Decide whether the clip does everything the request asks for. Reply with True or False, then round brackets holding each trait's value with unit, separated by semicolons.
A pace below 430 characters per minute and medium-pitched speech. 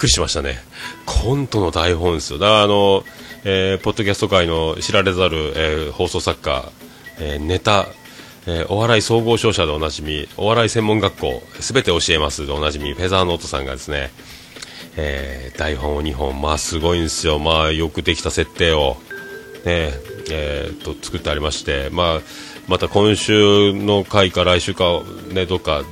False (335 characters per minute; 90 Hz)